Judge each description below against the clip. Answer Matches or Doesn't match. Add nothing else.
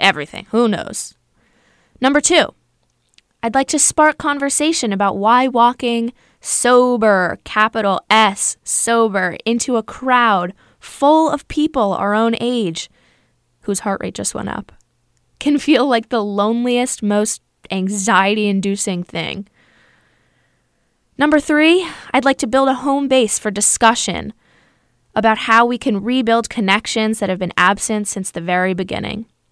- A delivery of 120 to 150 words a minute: Matches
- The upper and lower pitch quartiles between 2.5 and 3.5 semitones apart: Doesn't match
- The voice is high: Matches